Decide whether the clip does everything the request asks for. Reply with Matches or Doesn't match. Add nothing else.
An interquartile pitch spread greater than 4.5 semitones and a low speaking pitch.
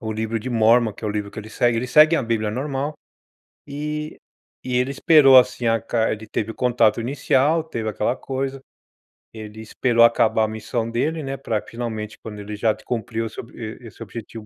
Doesn't match